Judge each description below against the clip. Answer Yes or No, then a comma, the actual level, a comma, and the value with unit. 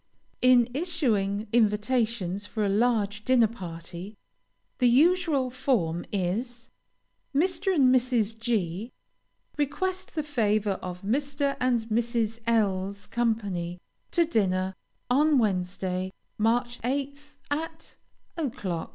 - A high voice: Yes, high, 230 Hz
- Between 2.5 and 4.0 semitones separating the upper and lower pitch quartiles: No, average, 5.2 semitones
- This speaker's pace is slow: Yes, slow, 110 wpm